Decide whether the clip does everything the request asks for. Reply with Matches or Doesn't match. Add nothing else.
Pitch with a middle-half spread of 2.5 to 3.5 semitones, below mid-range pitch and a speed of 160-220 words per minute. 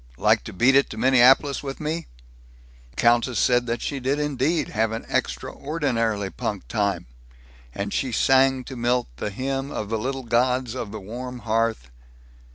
Matches